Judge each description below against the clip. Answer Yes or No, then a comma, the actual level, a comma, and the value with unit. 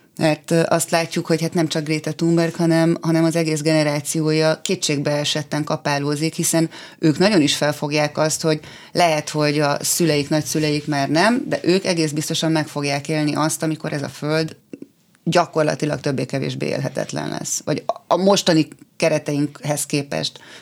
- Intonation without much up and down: Yes, narrow, 1.8 semitones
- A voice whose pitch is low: No, medium, 155 Hz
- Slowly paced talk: No, average, 150 wpm